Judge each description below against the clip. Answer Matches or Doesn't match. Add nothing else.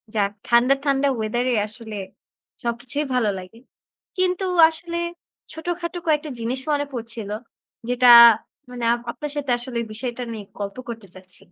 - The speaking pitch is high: Matches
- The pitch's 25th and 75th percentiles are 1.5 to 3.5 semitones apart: Doesn't match